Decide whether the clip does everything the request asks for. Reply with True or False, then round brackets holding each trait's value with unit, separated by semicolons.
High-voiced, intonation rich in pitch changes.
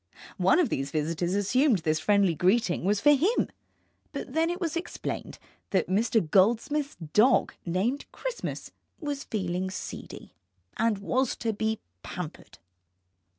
True (220 Hz; 7.1 semitones)